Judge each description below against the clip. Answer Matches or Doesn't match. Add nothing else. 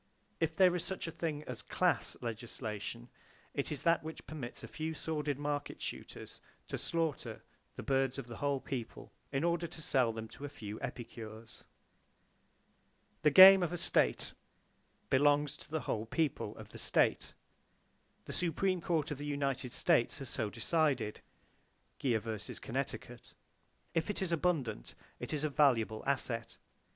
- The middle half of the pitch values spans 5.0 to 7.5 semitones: Matches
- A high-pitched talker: Doesn't match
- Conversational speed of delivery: Matches